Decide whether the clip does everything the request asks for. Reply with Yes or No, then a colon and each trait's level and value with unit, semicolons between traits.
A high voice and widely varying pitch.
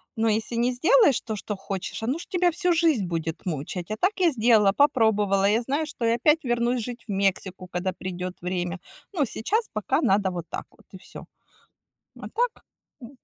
Yes: high, 225 Hz; wide, 6.8 semitones